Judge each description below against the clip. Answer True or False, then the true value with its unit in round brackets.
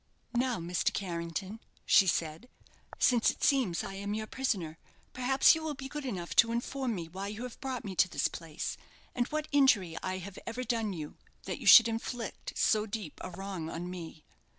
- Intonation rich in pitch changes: True (5.8 semitones)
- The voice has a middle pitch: False (210 Hz)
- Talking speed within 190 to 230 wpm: True (195 wpm)